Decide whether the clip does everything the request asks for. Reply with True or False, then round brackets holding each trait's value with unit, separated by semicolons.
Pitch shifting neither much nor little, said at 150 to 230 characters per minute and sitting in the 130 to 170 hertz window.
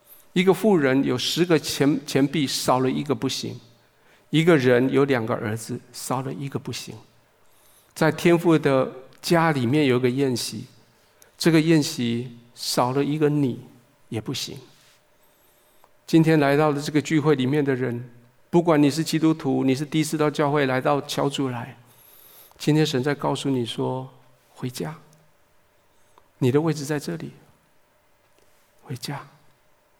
True (3.4 semitones; 210 characters per minute; 140 Hz)